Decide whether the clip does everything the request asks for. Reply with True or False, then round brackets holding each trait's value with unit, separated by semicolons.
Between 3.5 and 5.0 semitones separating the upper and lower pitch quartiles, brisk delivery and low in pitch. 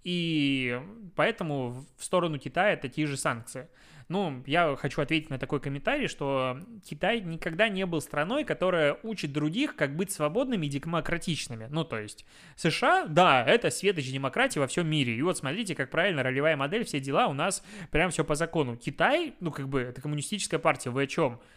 False (4.7 semitones; 185 wpm; 155 Hz)